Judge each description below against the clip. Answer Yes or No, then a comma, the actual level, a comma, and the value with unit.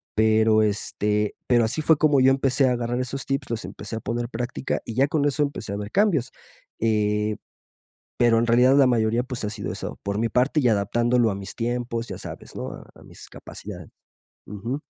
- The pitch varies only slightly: No, average, 3.2 semitones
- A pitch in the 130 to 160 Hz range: No, low, 120 Hz